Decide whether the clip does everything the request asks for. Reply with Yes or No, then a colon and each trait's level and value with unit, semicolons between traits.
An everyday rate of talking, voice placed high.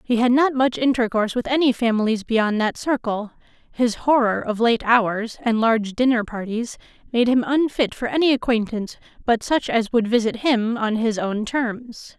Yes: average, 175 wpm; high, 235 Hz